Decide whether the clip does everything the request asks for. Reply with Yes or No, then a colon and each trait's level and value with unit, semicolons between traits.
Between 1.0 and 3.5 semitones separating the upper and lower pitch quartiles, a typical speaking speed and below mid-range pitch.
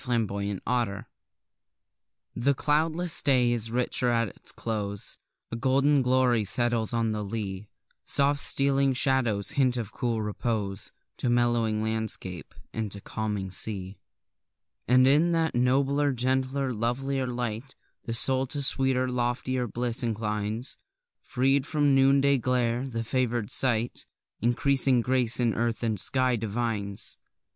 No: average, 3.1 semitones; slow, 130 wpm; low, 120 Hz